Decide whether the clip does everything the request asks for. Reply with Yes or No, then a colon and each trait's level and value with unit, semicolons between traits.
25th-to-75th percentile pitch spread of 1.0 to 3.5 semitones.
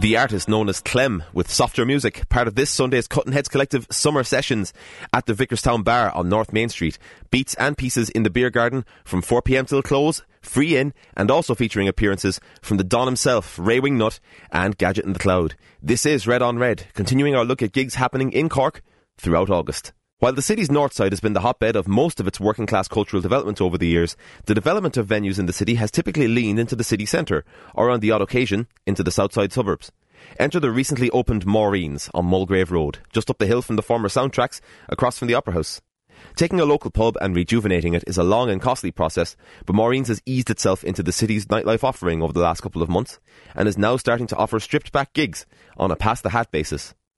No: average, 4.5 semitones